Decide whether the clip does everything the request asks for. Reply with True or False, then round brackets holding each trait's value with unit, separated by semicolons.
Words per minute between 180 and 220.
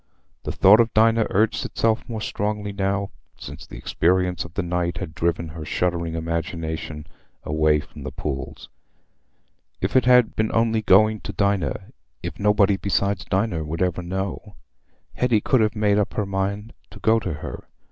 False (160 wpm)